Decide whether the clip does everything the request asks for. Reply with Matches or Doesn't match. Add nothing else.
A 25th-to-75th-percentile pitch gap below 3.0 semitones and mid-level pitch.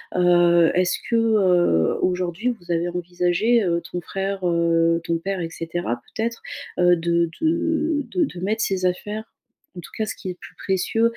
Doesn't match